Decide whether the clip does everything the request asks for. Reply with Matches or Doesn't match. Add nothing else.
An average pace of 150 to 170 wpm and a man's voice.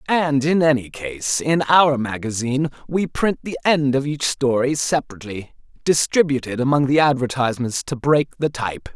Matches